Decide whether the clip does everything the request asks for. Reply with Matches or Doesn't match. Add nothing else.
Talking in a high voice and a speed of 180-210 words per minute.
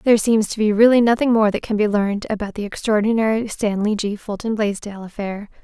Matches